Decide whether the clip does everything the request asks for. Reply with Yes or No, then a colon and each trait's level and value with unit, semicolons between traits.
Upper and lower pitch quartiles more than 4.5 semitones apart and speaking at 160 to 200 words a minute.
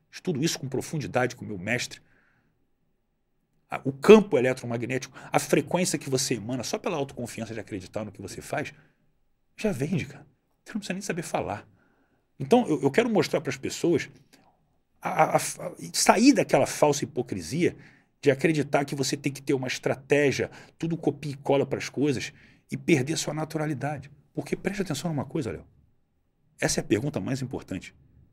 No: average, 4.2 semitones; average, 170 wpm